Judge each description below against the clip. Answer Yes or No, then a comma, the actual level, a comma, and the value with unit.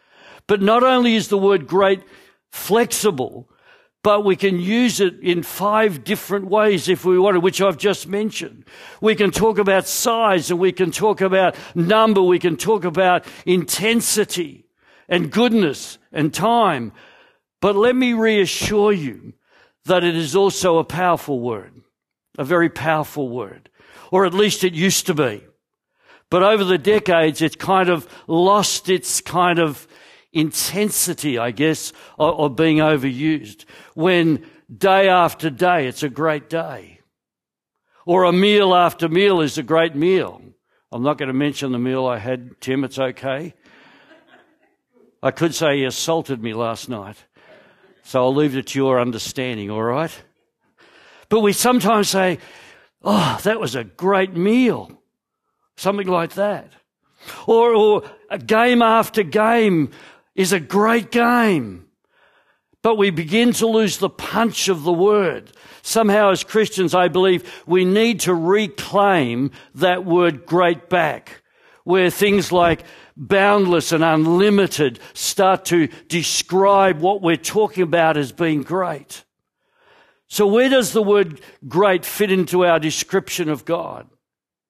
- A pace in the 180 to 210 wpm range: No, average, 145 wpm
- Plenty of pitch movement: No, average, 4.7 semitones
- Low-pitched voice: No, medium, 185 Hz